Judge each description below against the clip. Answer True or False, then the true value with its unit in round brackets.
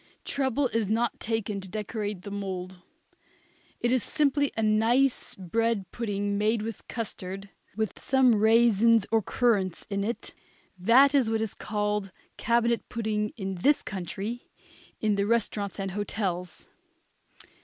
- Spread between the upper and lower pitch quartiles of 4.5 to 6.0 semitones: False (2.8 semitones)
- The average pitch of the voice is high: True (215 Hz)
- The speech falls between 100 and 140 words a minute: True (135 wpm)